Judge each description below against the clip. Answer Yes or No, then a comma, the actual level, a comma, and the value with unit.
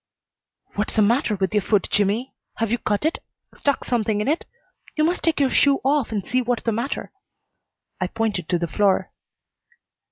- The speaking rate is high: No, average, 185 wpm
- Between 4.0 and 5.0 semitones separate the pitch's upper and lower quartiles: Yes, average, 4.5 semitones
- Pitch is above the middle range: Yes, high, 225 Hz